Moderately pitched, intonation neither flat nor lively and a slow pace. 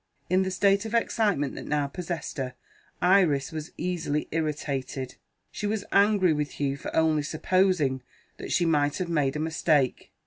No: medium, 160 Hz; average, 4.3 semitones; average, 165 wpm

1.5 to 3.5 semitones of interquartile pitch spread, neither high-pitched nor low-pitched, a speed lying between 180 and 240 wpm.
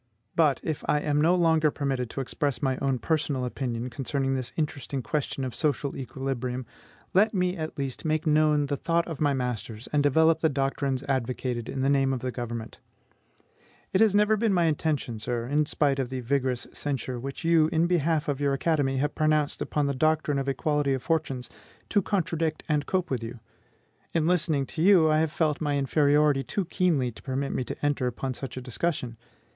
Yes: average, 3.1 semitones; medium, 145 Hz; average, 195 wpm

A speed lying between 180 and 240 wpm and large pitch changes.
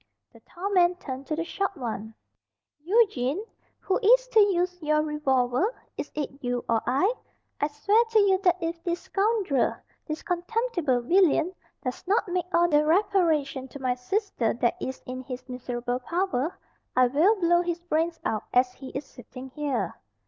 No: average, 170 wpm; wide, 6.6 semitones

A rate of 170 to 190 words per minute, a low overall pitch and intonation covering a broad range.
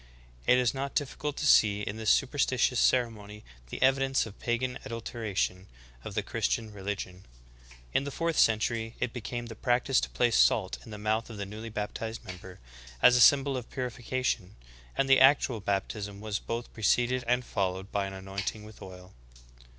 No: average, 180 wpm; low, 115 Hz; average, 3.7 semitones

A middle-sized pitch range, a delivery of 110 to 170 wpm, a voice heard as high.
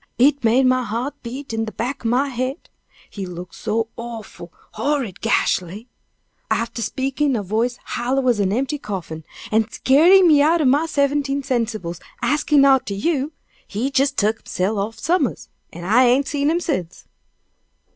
Yes: average, 4.4 semitones; average, 165 wpm; very high, 250 Hz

